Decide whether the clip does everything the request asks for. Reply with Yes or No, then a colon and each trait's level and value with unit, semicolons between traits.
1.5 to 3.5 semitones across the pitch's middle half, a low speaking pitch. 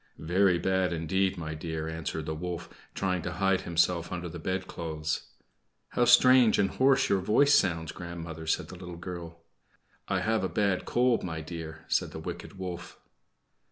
Yes: average, 2.8 semitones; very low, 90 Hz